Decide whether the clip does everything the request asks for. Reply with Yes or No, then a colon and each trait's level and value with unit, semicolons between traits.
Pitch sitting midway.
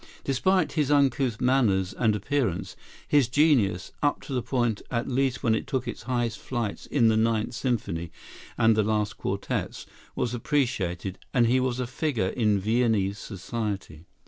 No: low, 120 Hz